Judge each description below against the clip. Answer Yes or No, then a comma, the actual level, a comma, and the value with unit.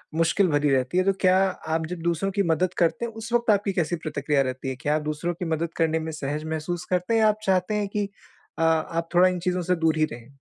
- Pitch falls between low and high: Yes, medium, 170 Hz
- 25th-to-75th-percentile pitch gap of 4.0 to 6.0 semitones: No, average, 3.2 semitones